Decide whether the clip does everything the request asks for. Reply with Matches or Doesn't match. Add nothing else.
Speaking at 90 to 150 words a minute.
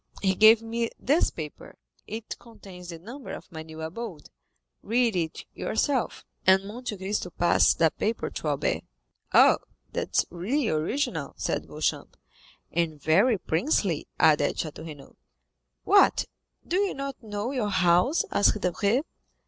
Matches